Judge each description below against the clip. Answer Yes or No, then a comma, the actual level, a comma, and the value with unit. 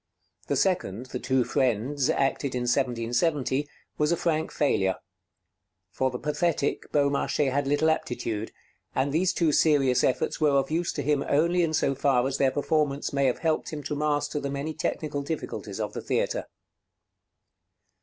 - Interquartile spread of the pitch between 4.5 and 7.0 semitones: No, average, 2.8 semitones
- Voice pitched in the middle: Yes, medium, 145 Hz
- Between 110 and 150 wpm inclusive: No, average, 160 wpm